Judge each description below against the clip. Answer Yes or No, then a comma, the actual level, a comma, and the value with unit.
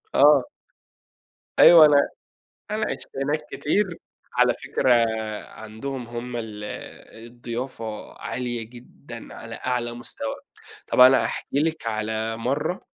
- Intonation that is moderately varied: Yes, average, 3.7 semitones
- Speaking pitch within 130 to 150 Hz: No, low, 120 Hz